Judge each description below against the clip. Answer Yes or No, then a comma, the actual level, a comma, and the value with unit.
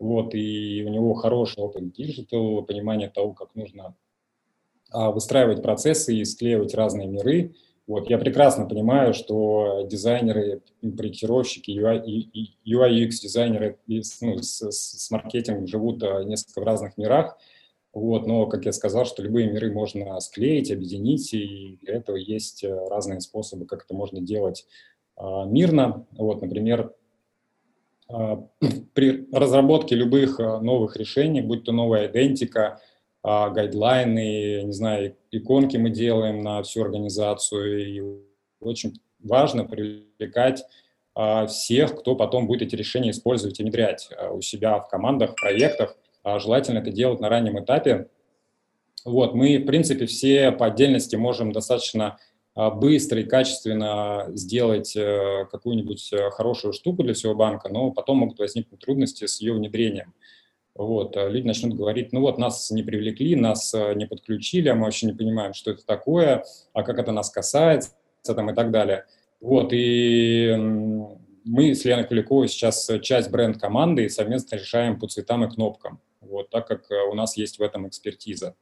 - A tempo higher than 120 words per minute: Yes, average, 140 wpm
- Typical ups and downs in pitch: No, narrow, 2.3 semitones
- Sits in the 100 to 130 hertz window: Yes, low, 110 Hz